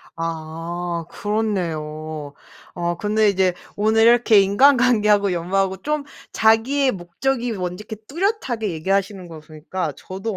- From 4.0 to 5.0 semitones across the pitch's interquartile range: Yes, average, 4.5 semitones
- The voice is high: Yes, high, 195 Hz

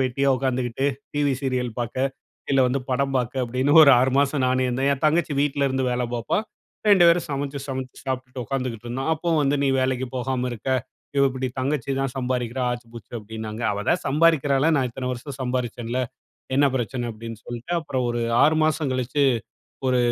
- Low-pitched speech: Yes, low, 130 Hz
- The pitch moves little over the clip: Yes, narrow, 2.1 semitones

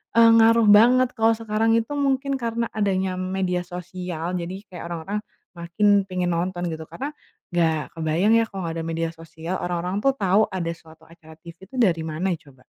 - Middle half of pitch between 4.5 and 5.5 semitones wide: Yes, average, 4.9 semitones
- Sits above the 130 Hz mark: Yes, medium, 185 Hz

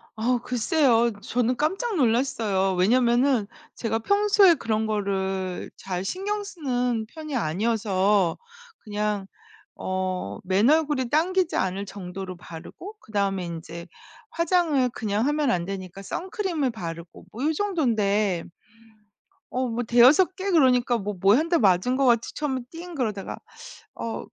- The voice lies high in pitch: Yes, high, 235 Hz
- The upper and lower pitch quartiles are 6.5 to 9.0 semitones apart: Yes, wide, 7.3 semitones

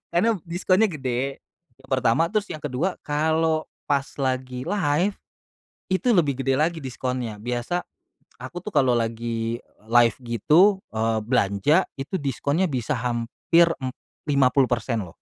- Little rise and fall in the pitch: No, wide, 5.5 semitones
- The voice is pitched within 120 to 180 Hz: Yes, low, 135 Hz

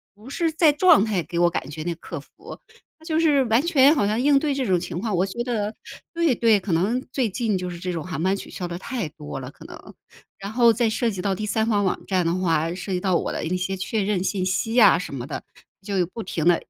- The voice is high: Yes, high, 200 Hz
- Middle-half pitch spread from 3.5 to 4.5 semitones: No, average, 5.1 semitones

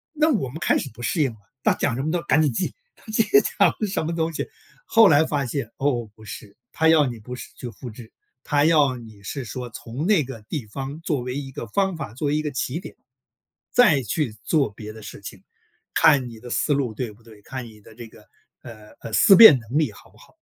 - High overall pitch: No, low, 130 Hz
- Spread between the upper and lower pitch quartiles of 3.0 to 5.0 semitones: No, wide, 5.5 semitones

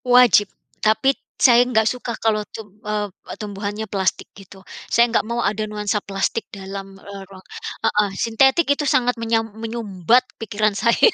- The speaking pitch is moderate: No, high, 215 Hz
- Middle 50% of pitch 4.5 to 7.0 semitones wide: No, average, 2.7 semitones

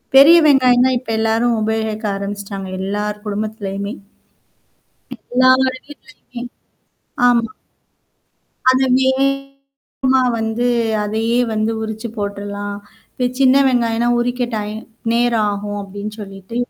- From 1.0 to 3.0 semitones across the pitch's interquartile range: No, average, 3.7 semitones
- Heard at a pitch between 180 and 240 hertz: Yes, high, 225 Hz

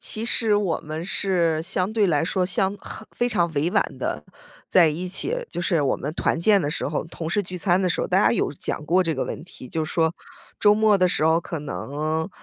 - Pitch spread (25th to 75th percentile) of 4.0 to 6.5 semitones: No, average, 3.6 semitones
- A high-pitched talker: No, medium, 175 Hz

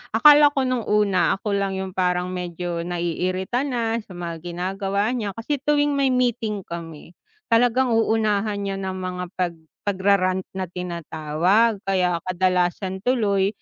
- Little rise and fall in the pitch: No, average, 3.9 semitones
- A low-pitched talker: No, high, 195 Hz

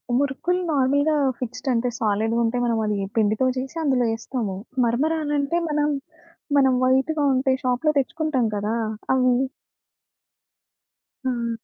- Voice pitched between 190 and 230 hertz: No, very high, 255 Hz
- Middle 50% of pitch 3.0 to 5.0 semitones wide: Yes, average, 3.5 semitones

